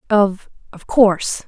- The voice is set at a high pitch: Yes, high, 200 Hz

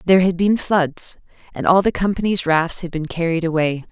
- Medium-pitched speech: Yes, medium, 175 Hz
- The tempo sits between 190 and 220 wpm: Yes, average, 200 wpm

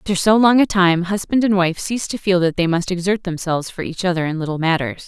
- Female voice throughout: Yes, female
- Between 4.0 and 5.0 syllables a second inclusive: No, 6.3 syllables/s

